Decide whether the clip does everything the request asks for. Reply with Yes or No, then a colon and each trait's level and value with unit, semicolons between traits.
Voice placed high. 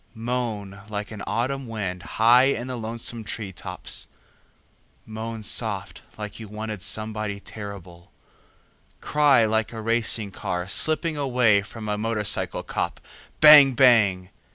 No: low, 110 Hz